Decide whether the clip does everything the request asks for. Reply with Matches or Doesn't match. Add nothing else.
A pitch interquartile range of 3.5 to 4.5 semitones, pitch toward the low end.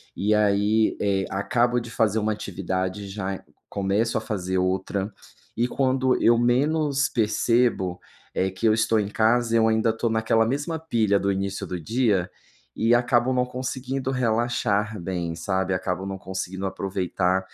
Matches